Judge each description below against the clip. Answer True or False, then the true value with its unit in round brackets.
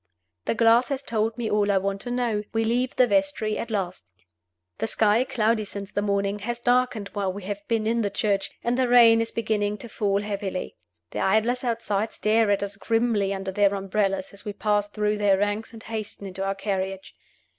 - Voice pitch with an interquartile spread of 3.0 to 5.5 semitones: False (2.4 semitones)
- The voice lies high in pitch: True (210 Hz)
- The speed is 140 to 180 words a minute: False (205 wpm)